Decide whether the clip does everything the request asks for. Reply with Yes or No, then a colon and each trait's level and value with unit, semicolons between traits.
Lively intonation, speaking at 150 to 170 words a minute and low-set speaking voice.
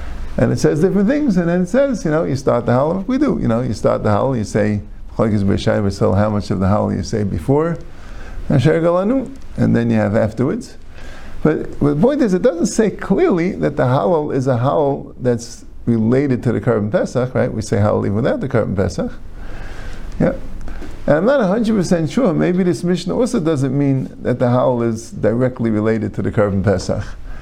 No: wide, 8.0 semitones; average, 195 wpm; low, 120 Hz